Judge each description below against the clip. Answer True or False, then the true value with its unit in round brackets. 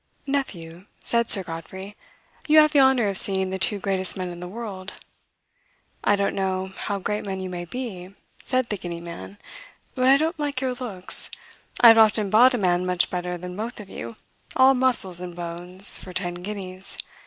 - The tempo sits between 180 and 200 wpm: True (190 wpm)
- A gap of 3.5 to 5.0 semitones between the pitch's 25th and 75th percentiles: True (4.5 semitones)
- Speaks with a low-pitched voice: False (195 Hz)